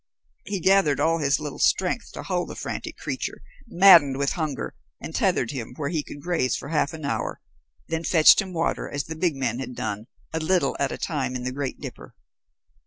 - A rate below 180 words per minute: No, fast, 205 wpm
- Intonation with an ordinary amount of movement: Yes, average, 3.5 semitones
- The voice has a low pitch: No, medium, 150 Hz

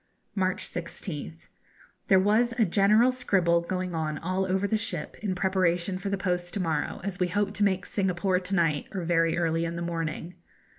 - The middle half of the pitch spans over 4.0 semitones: No, narrow, 2.6 semitones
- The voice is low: No, medium, 185 Hz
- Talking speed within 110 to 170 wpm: No, average, 190 wpm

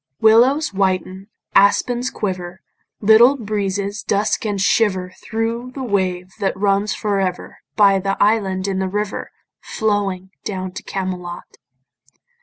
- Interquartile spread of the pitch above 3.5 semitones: No, narrow, 2.5 semitones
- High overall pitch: Yes, high, 200 Hz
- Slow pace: Yes, slow, 125 wpm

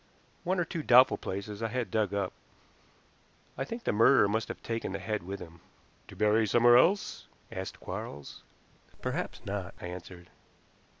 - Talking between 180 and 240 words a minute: No, average, 165 wpm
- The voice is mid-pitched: No, low, 105 Hz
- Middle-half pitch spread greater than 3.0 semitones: Yes, average, 4.1 semitones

